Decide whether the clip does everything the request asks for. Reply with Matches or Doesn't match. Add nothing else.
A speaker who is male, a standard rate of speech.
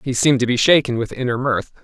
Doesn't match